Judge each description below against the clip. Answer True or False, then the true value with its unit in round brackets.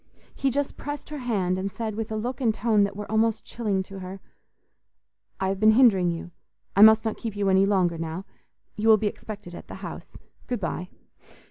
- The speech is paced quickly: True (210 wpm)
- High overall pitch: True (210 Hz)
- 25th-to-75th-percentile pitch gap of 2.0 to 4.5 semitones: True (2.9 semitones)